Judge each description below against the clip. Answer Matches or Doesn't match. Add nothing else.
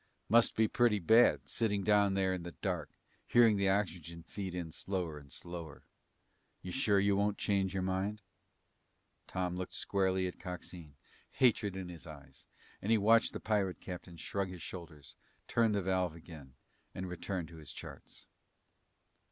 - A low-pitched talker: Matches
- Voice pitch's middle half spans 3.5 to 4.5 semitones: Doesn't match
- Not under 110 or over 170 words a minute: Matches